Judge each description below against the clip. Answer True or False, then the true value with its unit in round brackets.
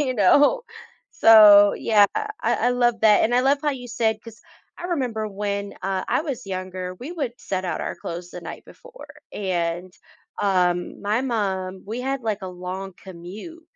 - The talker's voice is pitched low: False (210 Hz)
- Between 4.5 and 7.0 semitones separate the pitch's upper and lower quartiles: True (4.9 semitones)